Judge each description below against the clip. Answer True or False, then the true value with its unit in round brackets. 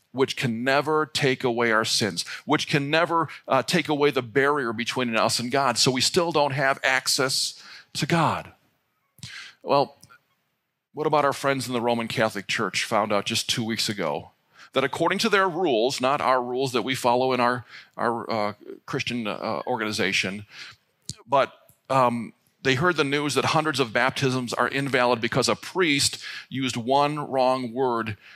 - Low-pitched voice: True (130 Hz)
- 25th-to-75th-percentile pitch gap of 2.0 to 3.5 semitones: True (3.2 semitones)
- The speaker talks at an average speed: True (170 wpm)